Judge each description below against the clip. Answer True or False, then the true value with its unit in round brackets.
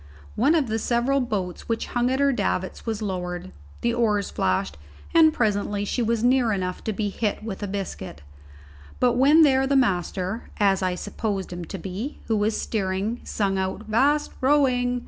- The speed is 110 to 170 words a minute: False (180 wpm)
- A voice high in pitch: True (220 Hz)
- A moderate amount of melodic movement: True (4.5 semitones)